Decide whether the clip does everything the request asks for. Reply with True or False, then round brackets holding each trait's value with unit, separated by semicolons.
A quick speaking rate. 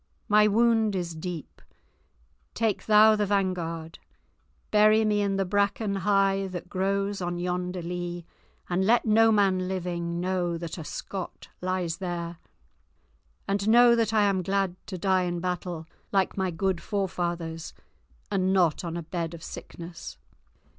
False (145 wpm)